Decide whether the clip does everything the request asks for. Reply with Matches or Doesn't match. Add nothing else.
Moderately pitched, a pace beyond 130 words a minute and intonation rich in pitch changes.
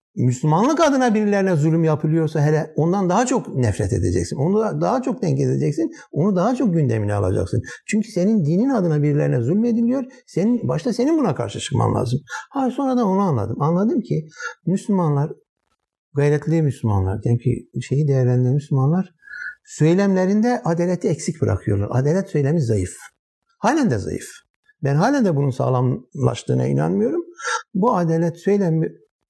Matches